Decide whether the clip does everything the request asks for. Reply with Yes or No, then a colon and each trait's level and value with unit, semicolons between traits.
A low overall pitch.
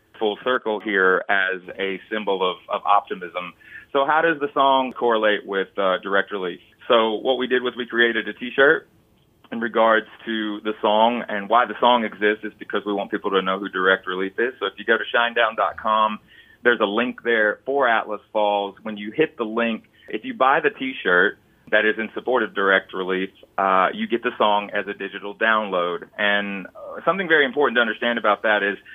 Yes: low, 105 Hz